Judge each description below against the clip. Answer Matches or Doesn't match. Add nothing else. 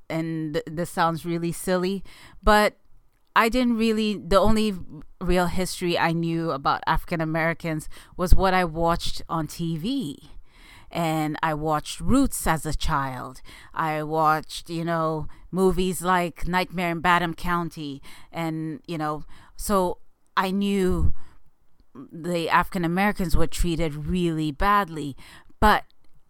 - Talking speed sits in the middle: Doesn't match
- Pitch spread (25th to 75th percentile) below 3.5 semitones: Matches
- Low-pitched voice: Doesn't match